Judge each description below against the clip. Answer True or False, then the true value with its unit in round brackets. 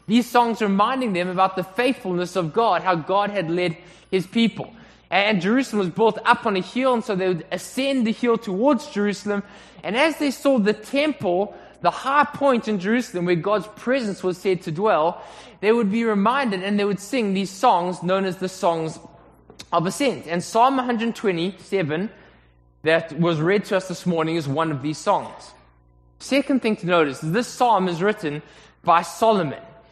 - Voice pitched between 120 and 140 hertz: False (195 Hz)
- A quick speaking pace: False (185 wpm)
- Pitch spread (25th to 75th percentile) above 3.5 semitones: True (4.6 semitones)